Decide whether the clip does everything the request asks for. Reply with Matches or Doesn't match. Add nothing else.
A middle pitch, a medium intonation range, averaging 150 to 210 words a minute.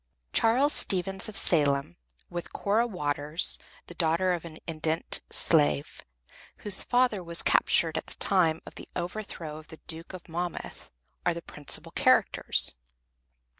Doesn't match